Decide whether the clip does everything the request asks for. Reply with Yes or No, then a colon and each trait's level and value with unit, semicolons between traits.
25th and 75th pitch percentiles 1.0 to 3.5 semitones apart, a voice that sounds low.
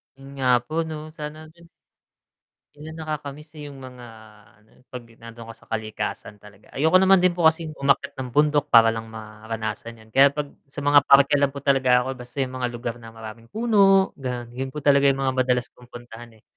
No: average, 4.3 semitones; low, 130 Hz